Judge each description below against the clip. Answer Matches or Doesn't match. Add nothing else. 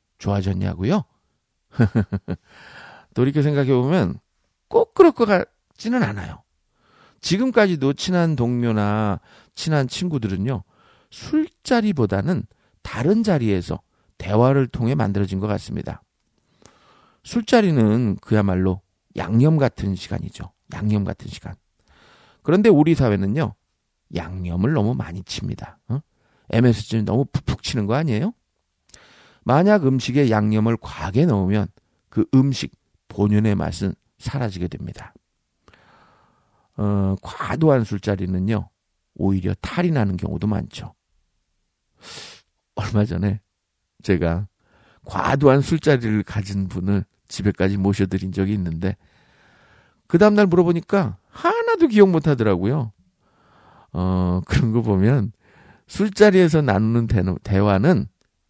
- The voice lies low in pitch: Matches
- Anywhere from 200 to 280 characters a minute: Matches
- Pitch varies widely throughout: Matches